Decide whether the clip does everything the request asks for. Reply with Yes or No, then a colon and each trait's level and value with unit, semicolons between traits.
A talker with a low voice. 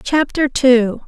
No: very high, 260 Hz